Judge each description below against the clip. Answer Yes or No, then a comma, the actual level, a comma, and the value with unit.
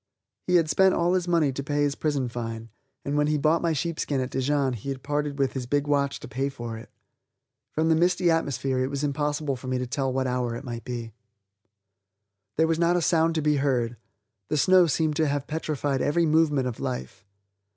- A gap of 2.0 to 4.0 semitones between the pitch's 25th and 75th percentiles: Yes, average, 3.5 semitones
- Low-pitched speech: No, medium, 145 Hz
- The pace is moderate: No, fast, 215 wpm